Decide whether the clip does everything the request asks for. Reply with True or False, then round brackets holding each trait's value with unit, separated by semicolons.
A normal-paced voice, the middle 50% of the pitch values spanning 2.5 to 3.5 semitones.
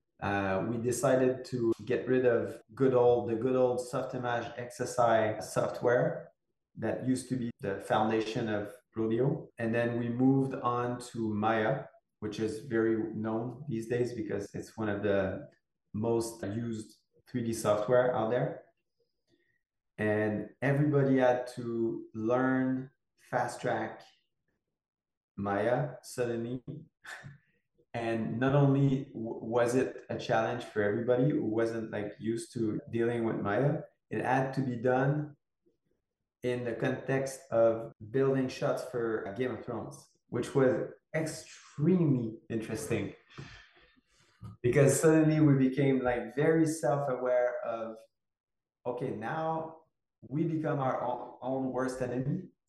False (125 wpm; 3.1 semitones)